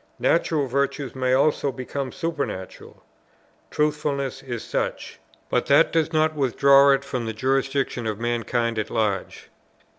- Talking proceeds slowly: Yes, slow, 130 wpm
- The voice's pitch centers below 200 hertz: Yes, low, 135 Hz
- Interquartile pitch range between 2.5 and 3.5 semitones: Yes, average, 3.1 semitones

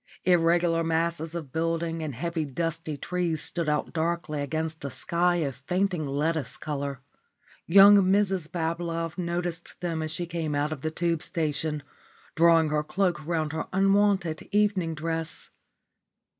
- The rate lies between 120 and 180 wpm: Yes, average, 145 wpm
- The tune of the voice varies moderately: No, narrow, 1.9 semitones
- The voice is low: No, medium, 165 Hz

